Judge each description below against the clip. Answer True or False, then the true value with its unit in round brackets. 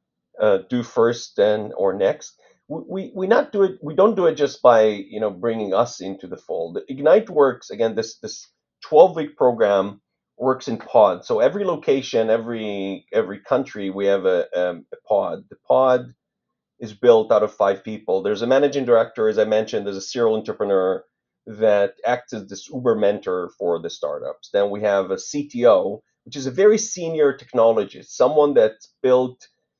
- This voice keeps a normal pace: True (180 wpm)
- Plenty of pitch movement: True (7.5 semitones)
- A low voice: True (120 Hz)